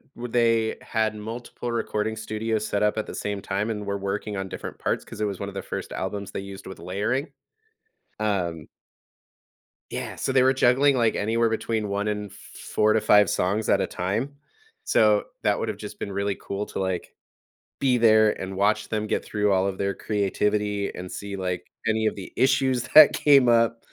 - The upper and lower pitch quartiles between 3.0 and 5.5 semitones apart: No, narrow, 2.4 semitones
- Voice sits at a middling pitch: No, low, 105 Hz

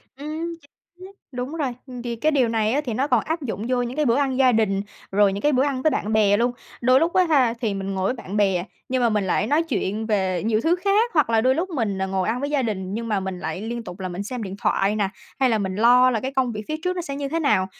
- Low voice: No, high, 235 Hz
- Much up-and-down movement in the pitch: Yes, wide, 5.7 semitones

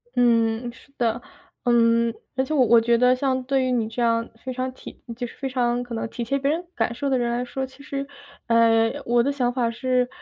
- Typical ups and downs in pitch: No, narrow, 1.9 semitones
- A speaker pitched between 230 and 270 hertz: Yes, high, 245 Hz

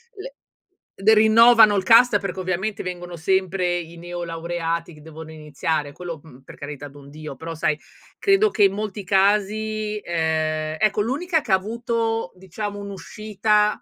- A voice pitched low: No, high, 190 Hz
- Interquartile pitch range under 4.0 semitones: No, average, 4.8 semitones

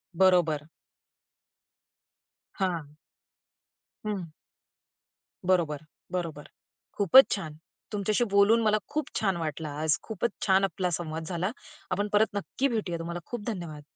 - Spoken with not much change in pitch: No, average, 4.2 semitones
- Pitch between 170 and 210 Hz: Yes, medium, 185 Hz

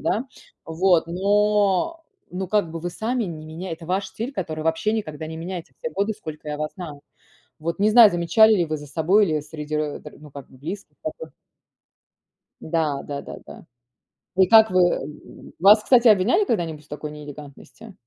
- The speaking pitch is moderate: Yes, medium, 175 Hz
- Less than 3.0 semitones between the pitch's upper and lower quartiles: No, average, 5.2 semitones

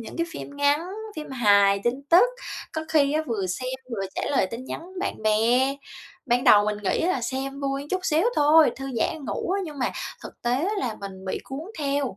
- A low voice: No, very high, 270 Hz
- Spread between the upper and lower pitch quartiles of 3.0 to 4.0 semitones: No, average, 4.8 semitones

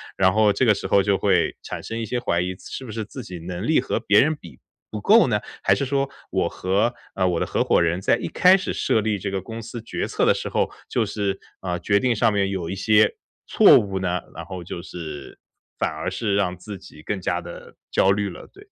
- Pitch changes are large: No, average, 3.6 semitones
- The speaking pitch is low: Yes, low, 100 Hz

